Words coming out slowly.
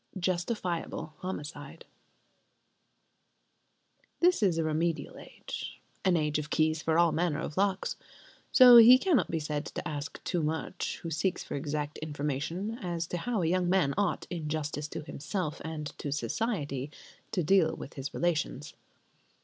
No: average, 150 wpm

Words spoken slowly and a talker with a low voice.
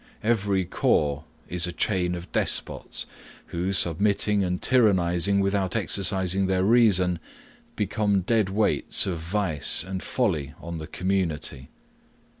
Yes: slow, 120 wpm; very low, 95 Hz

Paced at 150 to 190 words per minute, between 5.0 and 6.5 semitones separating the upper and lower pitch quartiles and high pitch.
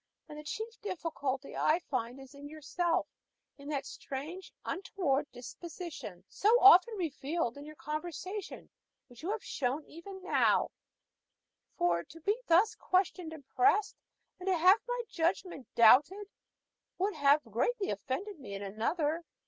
No: average, 140 wpm; wide, 5.5 semitones; very high, 320 Hz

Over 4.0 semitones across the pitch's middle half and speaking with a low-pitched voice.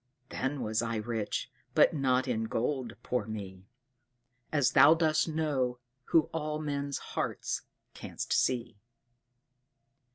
Yes: average, 4.8 semitones; low, 130 Hz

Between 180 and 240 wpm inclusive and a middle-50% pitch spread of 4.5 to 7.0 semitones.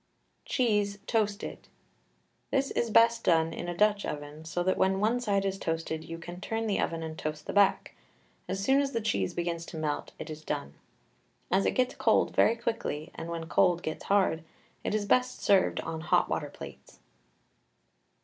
Yes: average, 185 wpm; average, 4.9 semitones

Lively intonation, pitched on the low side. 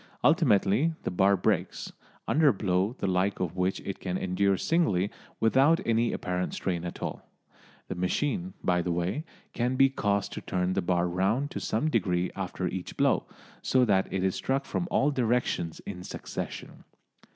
Yes: wide, 6.0 semitones; low, 100 Hz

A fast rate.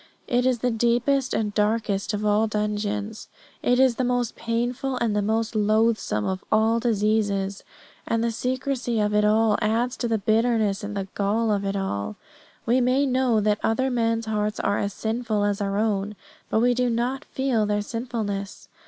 No: average, 180 wpm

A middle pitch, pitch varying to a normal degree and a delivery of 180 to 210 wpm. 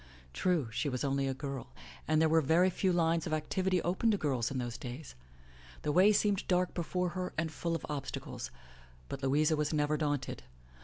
Yes: medium, 155 Hz; average, 4.4 semitones; average, 200 wpm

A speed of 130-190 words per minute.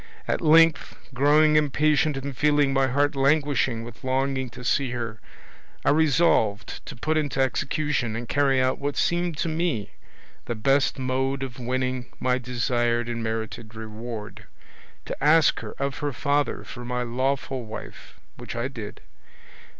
Yes: average, 150 wpm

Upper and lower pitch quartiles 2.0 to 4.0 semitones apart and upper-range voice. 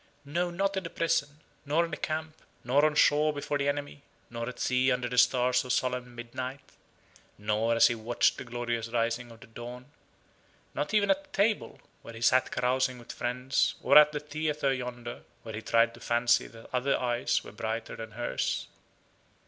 No: average, 3.7 semitones; low, 125 Hz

